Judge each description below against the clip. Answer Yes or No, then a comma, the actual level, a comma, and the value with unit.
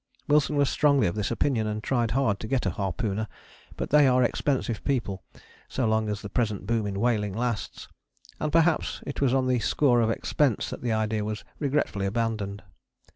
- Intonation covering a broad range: No, average, 4.1 semitones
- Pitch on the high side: No, low, 115 Hz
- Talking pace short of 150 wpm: No, average, 190 wpm